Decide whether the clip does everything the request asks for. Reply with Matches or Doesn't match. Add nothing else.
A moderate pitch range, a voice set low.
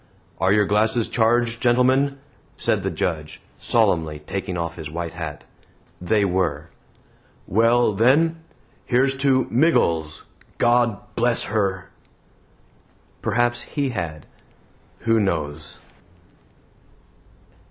Doesn't match